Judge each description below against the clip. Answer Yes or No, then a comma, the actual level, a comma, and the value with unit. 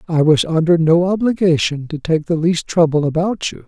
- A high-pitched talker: No, medium, 165 Hz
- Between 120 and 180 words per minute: No, average, 195 wpm